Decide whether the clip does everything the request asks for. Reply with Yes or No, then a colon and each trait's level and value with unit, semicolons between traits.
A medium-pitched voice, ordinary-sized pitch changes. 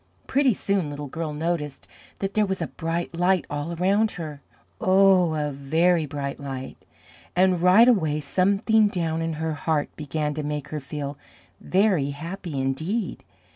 Yes: medium, 165 Hz; average, 4.2 semitones